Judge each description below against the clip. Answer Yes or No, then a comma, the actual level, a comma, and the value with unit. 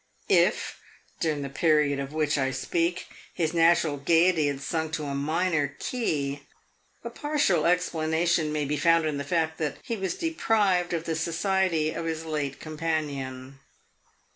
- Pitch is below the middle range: No, medium, 160 Hz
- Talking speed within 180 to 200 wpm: No, average, 155 wpm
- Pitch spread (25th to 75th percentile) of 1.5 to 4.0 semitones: Yes, average, 2.9 semitones